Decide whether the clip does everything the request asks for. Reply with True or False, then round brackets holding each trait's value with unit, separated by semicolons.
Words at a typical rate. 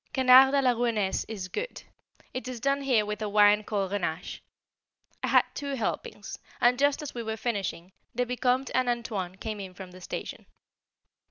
True (180 wpm)